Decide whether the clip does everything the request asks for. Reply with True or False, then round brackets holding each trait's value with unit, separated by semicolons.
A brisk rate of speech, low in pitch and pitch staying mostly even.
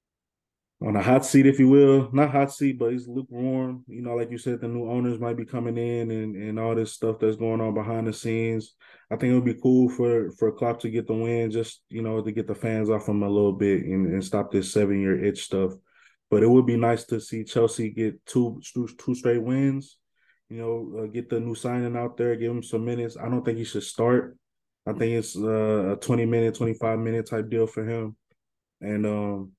True (235 wpm; 115 Hz; 1.6 semitones)